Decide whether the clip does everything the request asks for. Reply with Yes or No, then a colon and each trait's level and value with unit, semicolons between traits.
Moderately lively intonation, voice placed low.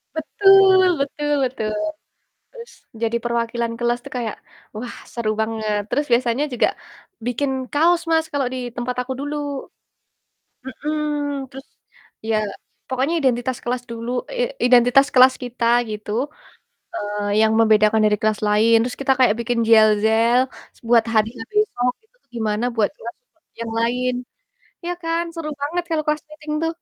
No: average, 4.4 semitones; high, 245 Hz